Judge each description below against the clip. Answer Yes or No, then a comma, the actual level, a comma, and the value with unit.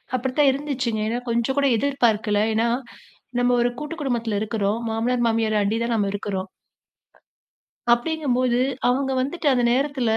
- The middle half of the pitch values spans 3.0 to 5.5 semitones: Yes, average, 3.3 semitones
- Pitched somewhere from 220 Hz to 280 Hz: Yes, high, 240 Hz